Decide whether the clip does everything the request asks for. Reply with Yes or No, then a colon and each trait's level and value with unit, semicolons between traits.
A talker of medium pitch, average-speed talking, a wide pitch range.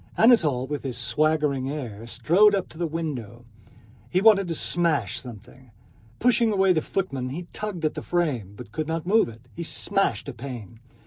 Yes: medium, 155 Hz; average, 180 wpm; wide, 6.3 semitones